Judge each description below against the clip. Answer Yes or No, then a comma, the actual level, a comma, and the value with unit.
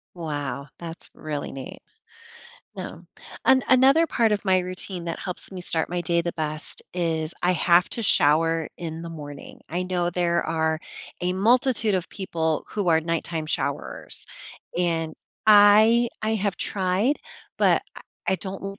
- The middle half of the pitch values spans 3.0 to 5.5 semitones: Yes, average, 3.6 semitones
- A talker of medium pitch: Yes, medium, 175 Hz